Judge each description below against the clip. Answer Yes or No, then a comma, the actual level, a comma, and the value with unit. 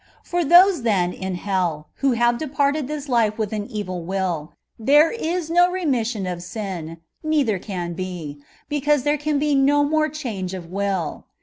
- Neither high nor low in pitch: No, high, 230 Hz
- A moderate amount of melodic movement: No, wide, 8.1 semitones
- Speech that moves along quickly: No, average, 175 wpm